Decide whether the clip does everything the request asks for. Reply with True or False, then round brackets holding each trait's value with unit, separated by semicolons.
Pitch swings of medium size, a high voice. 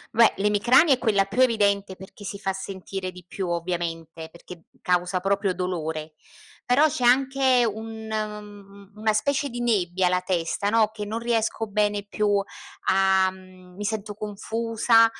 True (3.2 semitones; 205 Hz)